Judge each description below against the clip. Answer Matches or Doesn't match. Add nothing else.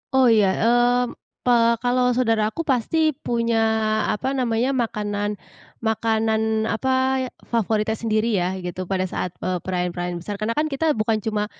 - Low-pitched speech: Doesn't match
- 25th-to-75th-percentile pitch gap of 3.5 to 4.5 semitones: Doesn't match